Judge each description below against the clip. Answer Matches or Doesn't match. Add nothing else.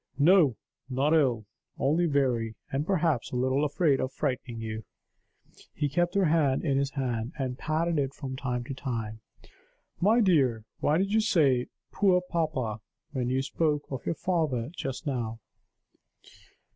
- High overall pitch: Doesn't match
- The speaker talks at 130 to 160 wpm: Matches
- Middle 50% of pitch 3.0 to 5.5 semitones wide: Matches